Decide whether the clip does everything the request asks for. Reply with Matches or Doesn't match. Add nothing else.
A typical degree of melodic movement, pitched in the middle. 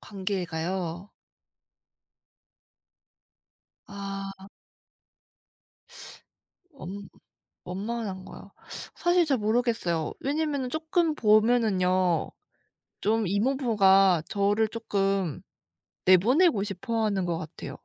Doesn't match